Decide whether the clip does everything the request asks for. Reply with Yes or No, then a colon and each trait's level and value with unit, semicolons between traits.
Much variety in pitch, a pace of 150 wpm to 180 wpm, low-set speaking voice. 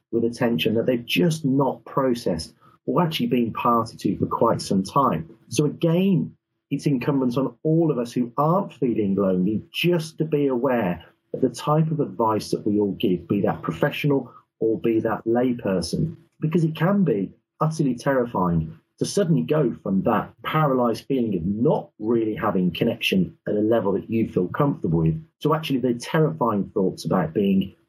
Yes: wide, 5.8 semitones; average, 175 wpm; low, 125 Hz